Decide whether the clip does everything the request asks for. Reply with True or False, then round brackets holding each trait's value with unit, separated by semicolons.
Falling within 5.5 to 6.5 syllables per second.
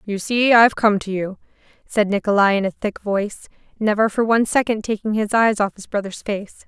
True (5.6 syllables/s)